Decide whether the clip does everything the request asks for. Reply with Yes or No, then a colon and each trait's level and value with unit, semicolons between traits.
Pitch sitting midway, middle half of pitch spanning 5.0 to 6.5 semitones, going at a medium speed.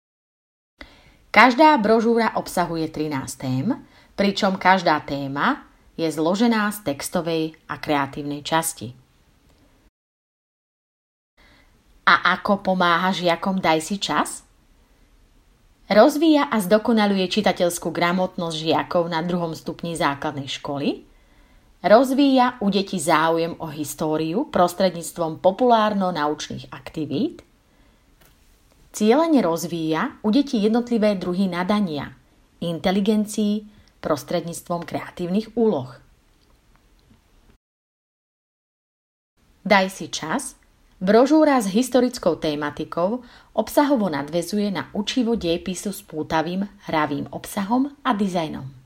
No: medium, 180 Hz; average, 5.3 semitones; slow, 85 wpm